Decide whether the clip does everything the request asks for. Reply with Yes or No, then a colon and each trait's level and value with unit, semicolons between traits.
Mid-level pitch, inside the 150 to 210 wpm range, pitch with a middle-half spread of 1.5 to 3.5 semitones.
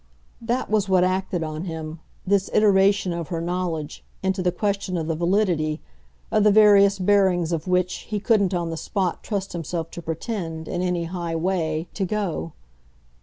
Yes: medium, 180 Hz; average, 170 wpm; average, 3.1 semitones